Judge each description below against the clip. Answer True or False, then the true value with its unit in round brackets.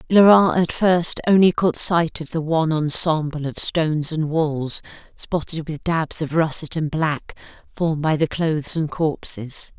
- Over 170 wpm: False (165 wpm)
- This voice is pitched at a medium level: True (160 Hz)